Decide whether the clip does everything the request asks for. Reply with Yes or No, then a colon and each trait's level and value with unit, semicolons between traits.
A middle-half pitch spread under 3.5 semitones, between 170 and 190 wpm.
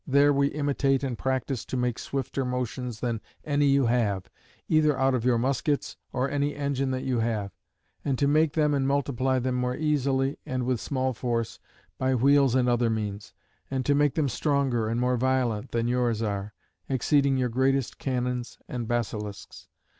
Yes: narrow, 2.6 semitones; average, 175 wpm